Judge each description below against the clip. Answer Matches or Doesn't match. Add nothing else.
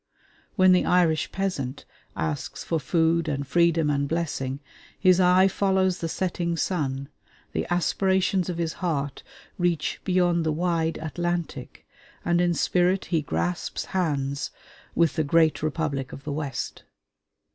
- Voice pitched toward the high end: Doesn't match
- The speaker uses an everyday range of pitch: Matches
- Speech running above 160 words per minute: Doesn't match